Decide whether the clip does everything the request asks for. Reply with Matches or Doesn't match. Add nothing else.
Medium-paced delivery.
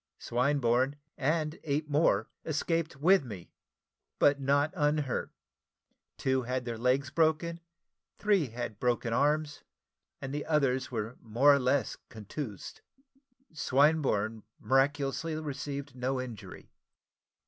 Doesn't match